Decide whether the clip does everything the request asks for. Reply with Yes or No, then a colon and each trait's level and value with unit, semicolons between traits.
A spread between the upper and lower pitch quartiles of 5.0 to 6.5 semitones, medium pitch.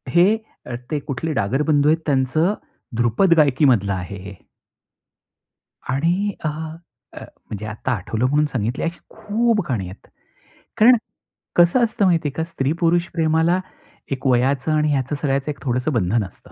Yes: wide, 5.4 semitones; medium, 145 Hz